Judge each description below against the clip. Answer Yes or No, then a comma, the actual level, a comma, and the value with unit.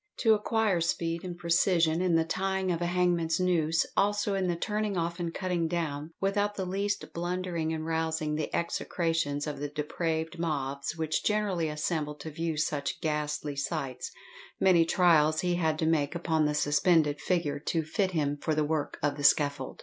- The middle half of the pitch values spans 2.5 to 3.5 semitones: Yes, average, 2.9 semitones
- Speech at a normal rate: Yes, average, 180 wpm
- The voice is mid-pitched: Yes, medium, 165 Hz